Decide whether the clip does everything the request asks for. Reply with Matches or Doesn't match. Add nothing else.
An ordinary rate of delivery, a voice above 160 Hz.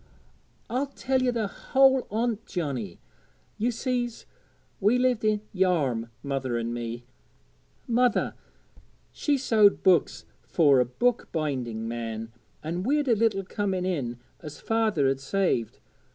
Doesn't match